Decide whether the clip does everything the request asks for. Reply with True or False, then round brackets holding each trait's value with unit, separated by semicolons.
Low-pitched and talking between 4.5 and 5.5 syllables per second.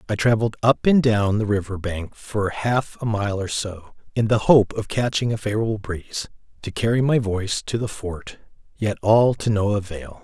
True (105 Hz; 5.0 syllables/s)